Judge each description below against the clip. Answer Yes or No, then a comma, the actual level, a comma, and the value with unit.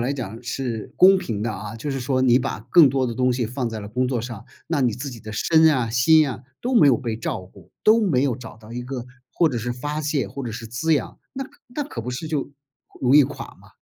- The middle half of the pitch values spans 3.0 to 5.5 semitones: Yes, average, 4.0 semitones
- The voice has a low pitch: Yes, low, 125 Hz